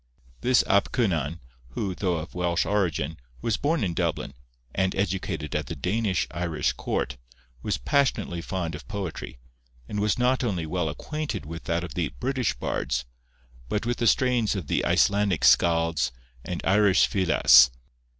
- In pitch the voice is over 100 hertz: No, very low, 90 Hz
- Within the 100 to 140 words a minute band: No, average, 155 wpm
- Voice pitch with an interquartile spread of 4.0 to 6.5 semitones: Yes, average, 4.3 semitones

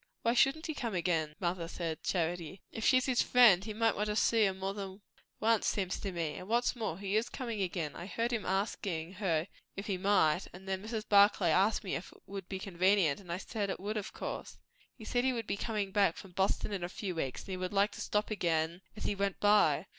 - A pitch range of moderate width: Yes, average, 3.2 semitones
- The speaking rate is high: Yes, fast, 245 wpm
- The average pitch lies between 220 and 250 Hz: No, high, 195 Hz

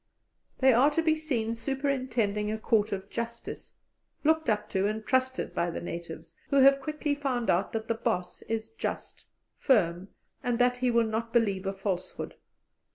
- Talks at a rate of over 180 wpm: No, average, 170 wpm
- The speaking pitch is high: Yes, high, 230 Hz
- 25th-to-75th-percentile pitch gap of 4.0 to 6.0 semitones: Yes, average, 4.3 semitones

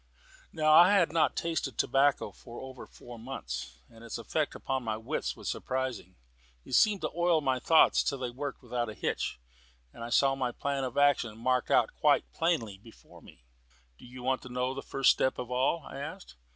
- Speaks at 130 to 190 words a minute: No, average, 200 wpm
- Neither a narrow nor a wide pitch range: Yes, average, 3.3 semitones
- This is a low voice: Yes, low, 130 Hz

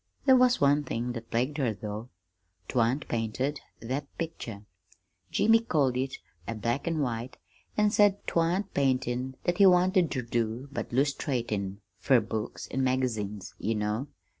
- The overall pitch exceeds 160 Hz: No, low, 130 Hz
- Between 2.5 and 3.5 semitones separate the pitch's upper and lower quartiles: No, average, 4.8 semitones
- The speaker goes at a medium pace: Yes, average, 150 wpm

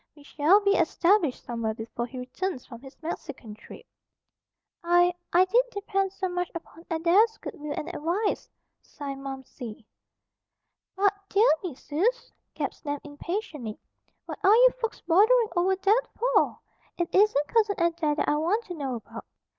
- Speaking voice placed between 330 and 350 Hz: Yes, very high, 345 Hz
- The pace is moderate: Yes, average, 155 wpm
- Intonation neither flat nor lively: No, wide, 5.8 semitones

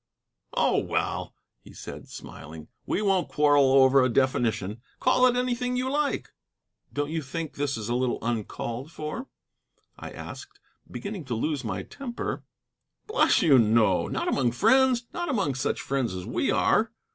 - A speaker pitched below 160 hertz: Yes, medium, 140 Hz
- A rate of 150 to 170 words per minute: Yes, average, 155 wpm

